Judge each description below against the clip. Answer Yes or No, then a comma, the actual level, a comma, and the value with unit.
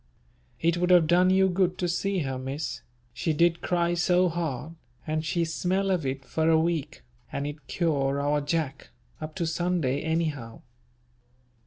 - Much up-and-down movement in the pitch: No, average, 3.3 semitones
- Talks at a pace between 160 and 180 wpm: Yes, average, 165 wpm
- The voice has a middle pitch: Yes, medium, 160 Hz